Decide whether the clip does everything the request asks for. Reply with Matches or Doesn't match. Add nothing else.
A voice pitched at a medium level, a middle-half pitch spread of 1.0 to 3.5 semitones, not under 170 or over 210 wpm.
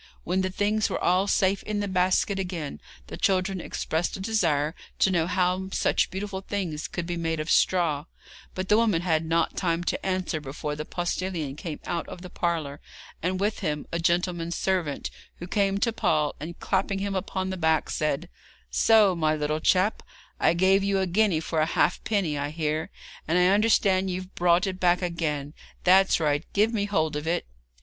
Matches